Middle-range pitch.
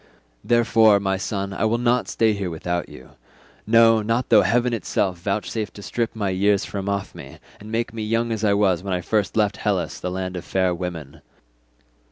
No: low, 100 Hz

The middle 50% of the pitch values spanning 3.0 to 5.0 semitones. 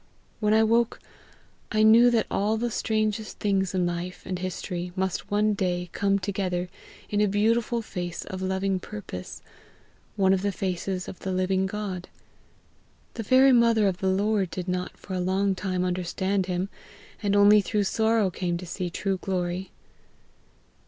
No: narrow, 2.4 semitones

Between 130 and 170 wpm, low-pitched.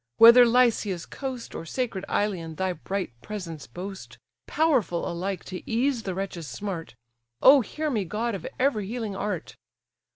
No: average, 150 wpm; high, 200 Hz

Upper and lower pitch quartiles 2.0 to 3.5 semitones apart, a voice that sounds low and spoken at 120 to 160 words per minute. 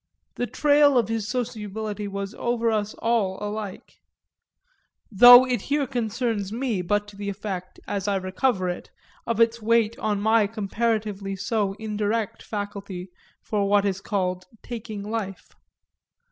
No: narrow, 2.6 semitones; high, 210 Hz; average, 140 wpm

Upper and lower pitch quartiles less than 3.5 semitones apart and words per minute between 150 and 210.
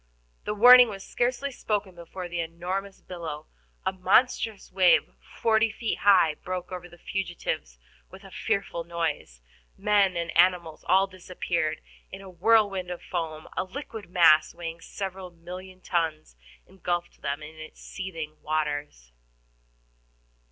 No: average, 3.0 semitones; slow, 135 wpm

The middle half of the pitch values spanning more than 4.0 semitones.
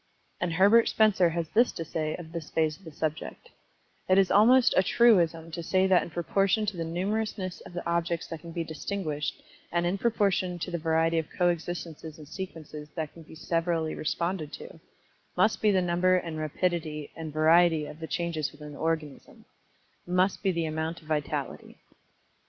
No: average, 2.7 semitones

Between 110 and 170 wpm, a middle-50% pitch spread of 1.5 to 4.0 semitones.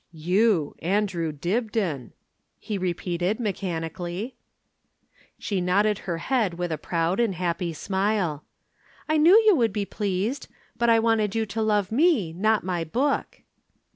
No: average, 140 wpm; average, 4.4 semitones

